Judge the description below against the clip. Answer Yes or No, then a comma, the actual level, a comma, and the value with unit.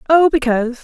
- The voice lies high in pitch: Yes, very high, 270 Hz